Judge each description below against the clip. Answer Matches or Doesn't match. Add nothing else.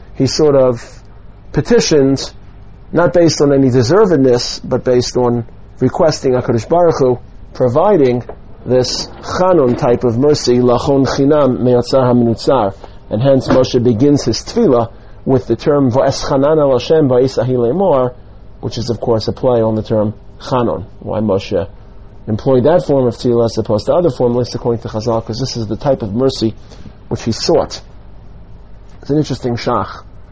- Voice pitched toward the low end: Matches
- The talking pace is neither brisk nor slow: Matches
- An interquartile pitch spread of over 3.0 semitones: Matches